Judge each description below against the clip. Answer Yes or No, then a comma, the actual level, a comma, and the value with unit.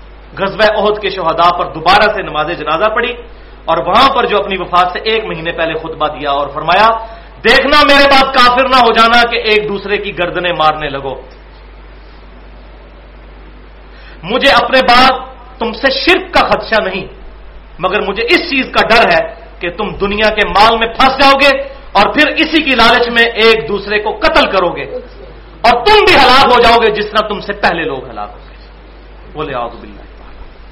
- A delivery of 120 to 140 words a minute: No, average, 180 wpm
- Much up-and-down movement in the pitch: Yes, wide, 6.7 semitones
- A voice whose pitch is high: Yes, high, 215 Hz